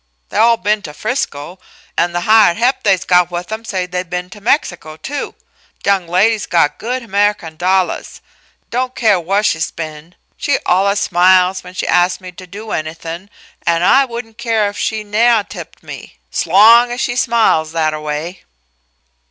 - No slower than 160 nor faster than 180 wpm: Yes, average, 175 wpm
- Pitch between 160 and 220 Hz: Yes, high, 190 Hz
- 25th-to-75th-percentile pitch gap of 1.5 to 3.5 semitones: No, average, 4.2 semitones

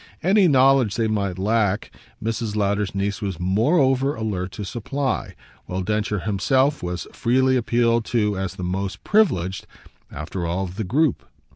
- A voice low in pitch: Yes, low, 105 Hz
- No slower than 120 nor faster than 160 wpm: Yes, average, 150 wpm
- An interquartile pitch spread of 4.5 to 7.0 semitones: Yes, average, 5.0 semitones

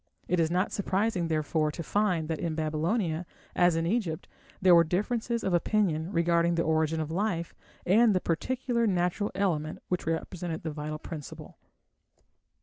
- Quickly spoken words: No, average, 155 wpm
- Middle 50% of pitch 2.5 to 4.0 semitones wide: Yes, average, 3.6 semitones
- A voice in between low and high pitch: Yes, medium, 170 Hz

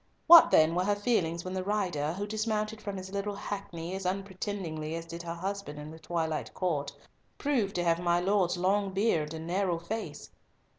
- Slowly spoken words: No, average, 190 wpm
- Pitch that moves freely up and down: No, average, 3.4 semitones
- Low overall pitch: No, medium, 185 Hz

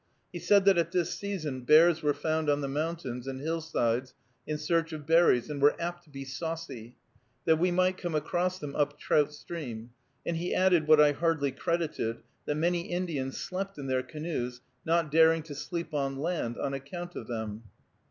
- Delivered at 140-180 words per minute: No, average, 190 wpm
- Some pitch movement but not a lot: Yes, average, 3.8 semitones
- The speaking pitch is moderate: Yes, medium, 155 Hz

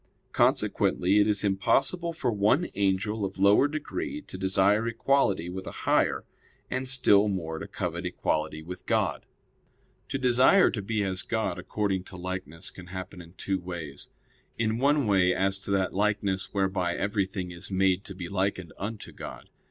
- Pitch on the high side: No, very low, 95 Hz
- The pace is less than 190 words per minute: Yes, average, 165 wpm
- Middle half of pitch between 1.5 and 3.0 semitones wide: Yes, average, 2.7 semitones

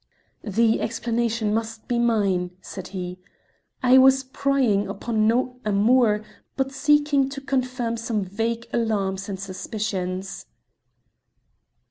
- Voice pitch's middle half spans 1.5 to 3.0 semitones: No, average, 4.0 semitones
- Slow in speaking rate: Yes, slow, 110 wpm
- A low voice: No, high, 225 Hz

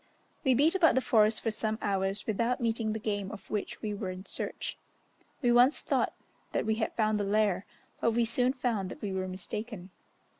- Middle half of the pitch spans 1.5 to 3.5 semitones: Yes, average, 2.9 semitones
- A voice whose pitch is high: Yes, high, 215 Hz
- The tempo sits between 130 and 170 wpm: No, average, 200 wpm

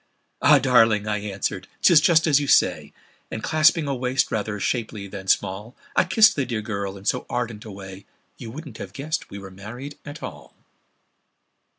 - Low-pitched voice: Yes, low, 115 Hz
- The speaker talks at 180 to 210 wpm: Yes, average, 185 wpm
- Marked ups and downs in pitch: Yes, wide, 6.0 semitones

